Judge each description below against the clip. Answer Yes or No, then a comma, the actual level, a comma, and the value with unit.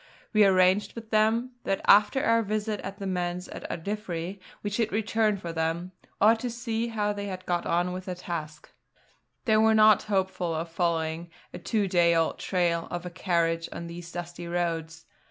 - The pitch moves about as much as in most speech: Yes, average, 3.8 semitones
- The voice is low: No, medium, 185 Hz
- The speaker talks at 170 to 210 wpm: Yes, average, 185 wpm